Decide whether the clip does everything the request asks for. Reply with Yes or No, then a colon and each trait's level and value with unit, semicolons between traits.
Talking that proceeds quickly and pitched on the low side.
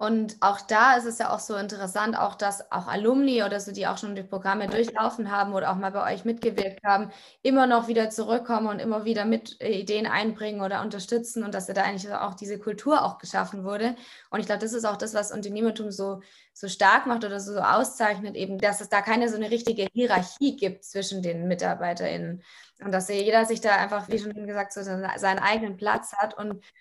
No: fast, 215 wpm; high, 205 Hz